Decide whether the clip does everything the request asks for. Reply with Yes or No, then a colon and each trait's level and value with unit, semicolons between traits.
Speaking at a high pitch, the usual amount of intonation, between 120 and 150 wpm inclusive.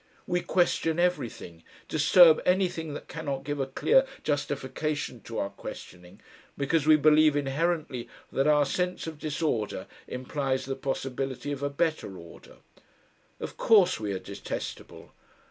No: medium, 145 Hz; average, 3.6 semitones; slow, 135 wpm